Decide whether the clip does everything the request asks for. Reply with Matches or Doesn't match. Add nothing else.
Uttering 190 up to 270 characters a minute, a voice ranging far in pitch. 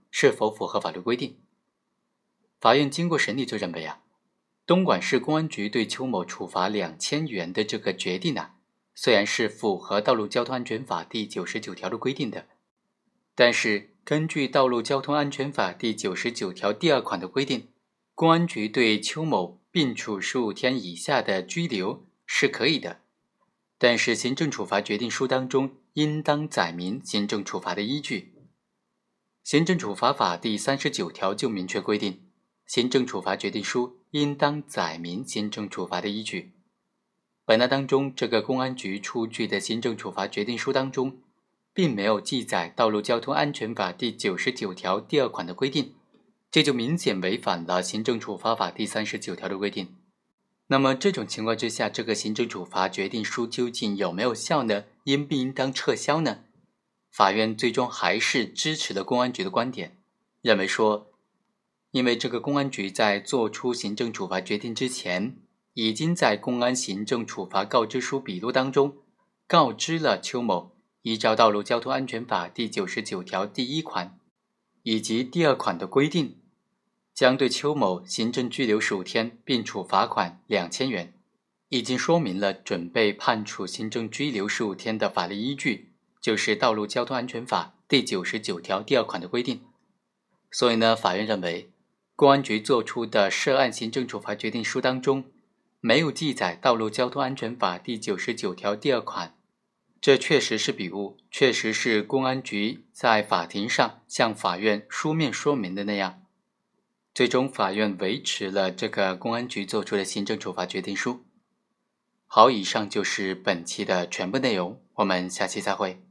Doesn't match